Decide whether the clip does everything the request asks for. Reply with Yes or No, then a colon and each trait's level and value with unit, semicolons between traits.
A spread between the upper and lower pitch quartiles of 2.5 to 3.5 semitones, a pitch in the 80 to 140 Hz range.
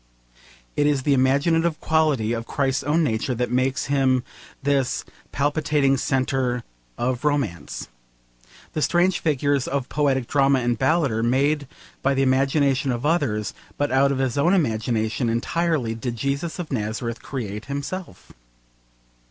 Yes: average, 3.0 semitones; low, 135 Hz